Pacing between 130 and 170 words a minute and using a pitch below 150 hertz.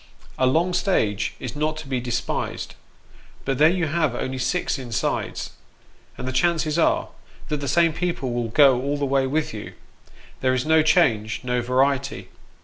Yes: average, 165 wpm; medium, 140 Hz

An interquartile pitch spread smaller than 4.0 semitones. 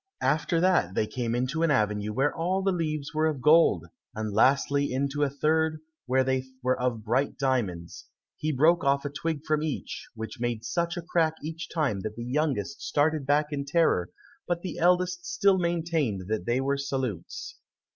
No: average, 4.7 semitones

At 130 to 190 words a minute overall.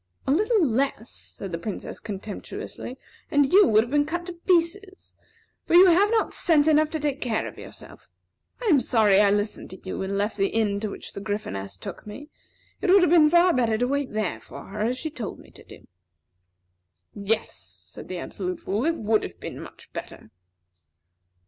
No: average, 200 wpm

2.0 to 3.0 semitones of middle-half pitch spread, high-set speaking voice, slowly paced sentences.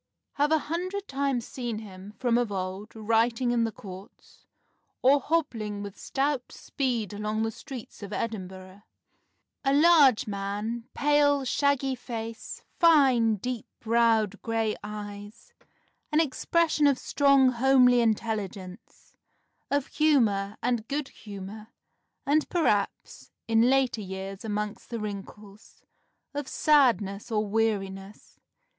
No: average, 4.6 semitones; high, 230 Hz; slow, 120 wpm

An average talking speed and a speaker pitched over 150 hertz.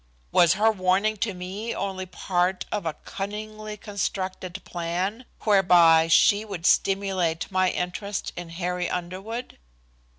No: slow, 125 wpm; high, 190 Hz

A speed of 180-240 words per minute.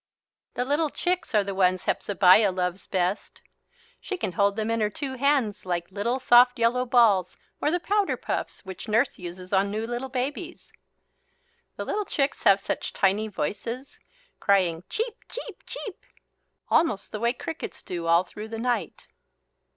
No: average, 165 wpm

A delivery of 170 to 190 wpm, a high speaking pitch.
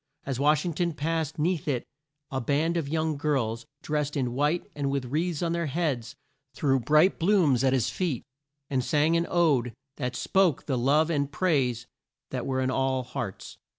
No: average, 185 wpm; medium, 145 Hz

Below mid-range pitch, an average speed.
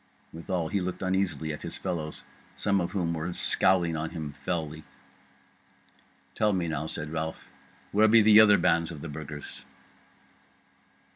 Yes: very low, 85 Hz; average, 150 wpm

